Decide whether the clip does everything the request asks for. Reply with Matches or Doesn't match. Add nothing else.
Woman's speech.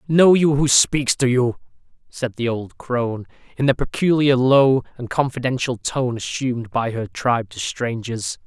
Doesn't match